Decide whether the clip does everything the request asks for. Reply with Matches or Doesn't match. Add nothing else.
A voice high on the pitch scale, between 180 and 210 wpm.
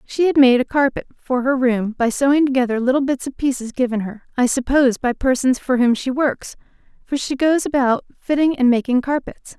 Matches